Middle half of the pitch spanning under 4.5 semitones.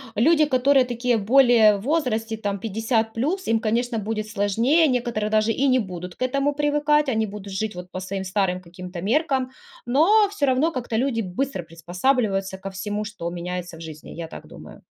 No: average, 5.3 semitones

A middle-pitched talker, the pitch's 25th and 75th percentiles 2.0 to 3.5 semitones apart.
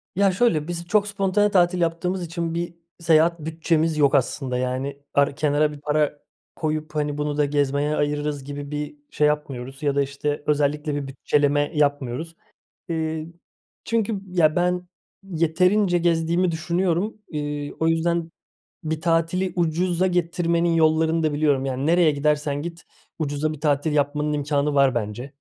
Yes: medium, 155 Hz; average, 2.8 semitones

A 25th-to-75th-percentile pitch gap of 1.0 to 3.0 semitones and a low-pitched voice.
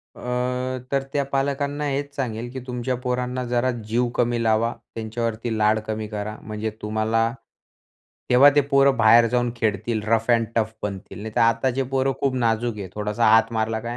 Yes: narrow, 2.6 semitones; low, 115 Hz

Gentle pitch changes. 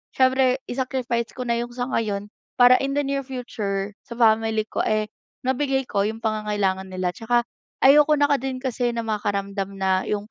No: average, 3.9 semitones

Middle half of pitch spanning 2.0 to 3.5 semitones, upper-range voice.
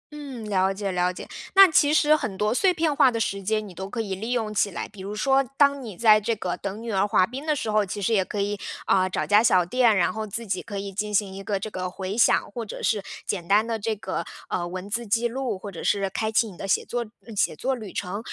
Yes: average, 3.1 semitones; high, 210 Hz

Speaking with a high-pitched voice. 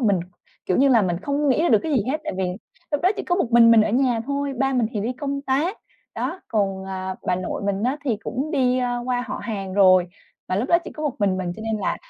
Yes: high, 240 Hz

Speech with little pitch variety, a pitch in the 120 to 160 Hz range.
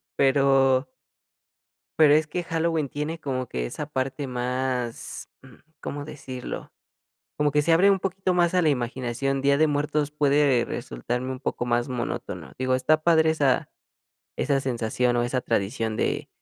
No: average, 3.2 semitones; low, 135 Hz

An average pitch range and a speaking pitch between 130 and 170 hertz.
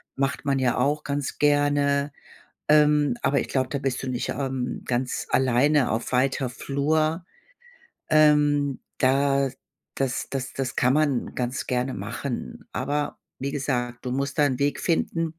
No: narrow, 2.2 semitones; medium, 140 Hz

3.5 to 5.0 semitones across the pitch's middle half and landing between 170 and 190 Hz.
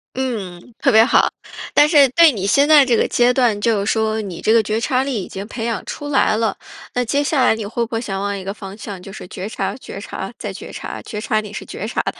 No: average, 3.9 semitones; high, 225 Hz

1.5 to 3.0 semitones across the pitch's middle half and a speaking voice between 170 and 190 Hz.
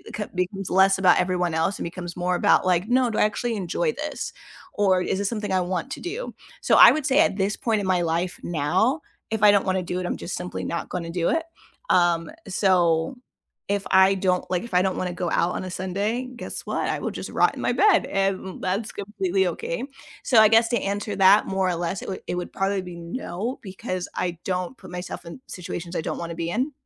Yes: average, 2.7 semitones; medium, 185 Hz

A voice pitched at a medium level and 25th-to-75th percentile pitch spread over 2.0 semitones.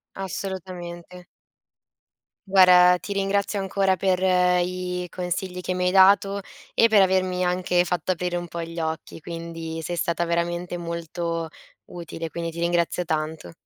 No: medium, 180 Hz; narrow, 1.6 semitones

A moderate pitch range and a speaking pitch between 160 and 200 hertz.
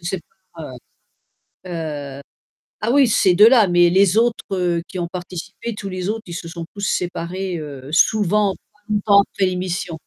Yes: average, 3.0 semitones; medium, 185 Hz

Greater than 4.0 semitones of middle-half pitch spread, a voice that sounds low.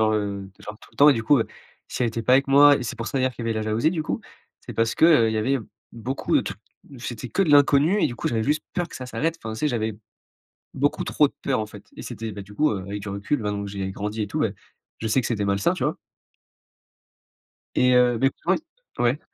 Yes: average, 4.5 semitones; low, 115 Hz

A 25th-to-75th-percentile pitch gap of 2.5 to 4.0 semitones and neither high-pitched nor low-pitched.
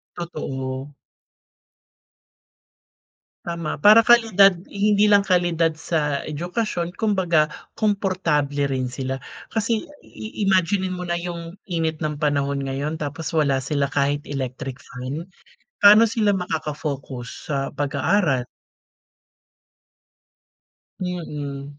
No: average, 4.9 semitones; medium, 160 Hz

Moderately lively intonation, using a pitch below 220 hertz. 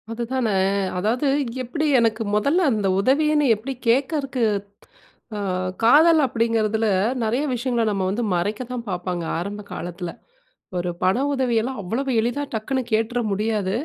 No: average, 4.0 semitones; high, 230 Hz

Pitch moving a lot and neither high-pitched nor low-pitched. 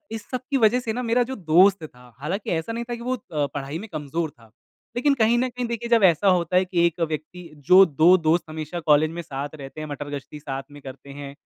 Yes: wide, 7.1 semitones; medium, 170 Hz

